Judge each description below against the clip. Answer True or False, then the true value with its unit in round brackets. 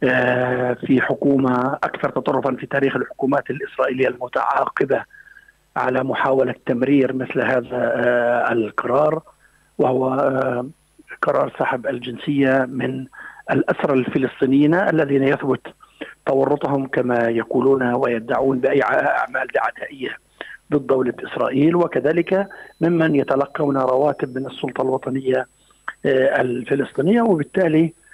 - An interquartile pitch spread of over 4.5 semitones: False (2.4 semitones)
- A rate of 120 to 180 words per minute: False (90 wpm)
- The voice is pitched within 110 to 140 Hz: True (135 Hz)